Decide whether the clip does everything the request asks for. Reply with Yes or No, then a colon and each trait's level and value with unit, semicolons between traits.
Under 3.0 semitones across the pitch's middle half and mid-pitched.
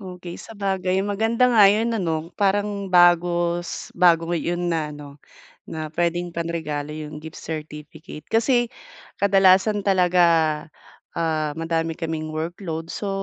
No: average, 3.3 semitones; medium, 175 Hz